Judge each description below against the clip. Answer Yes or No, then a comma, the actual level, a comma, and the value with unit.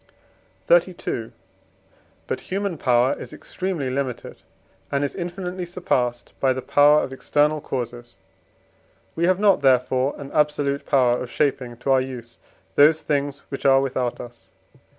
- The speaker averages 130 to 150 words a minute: Yes, average, 140 wpm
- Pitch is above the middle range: No, medium, 140 Hz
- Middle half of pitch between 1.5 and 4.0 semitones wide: Yes, average, 3.3 semitones